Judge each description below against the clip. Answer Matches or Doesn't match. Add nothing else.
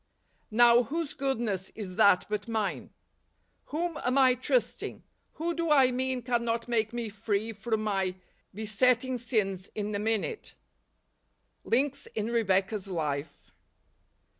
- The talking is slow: Matches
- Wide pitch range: Doesn't match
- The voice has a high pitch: Matches